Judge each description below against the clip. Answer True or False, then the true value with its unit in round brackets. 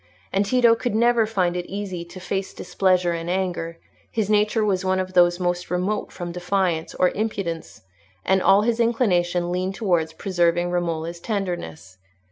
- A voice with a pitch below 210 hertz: True (185 Hz)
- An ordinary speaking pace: True (160 wpm)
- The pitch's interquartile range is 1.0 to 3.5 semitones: True (2.7 semitones)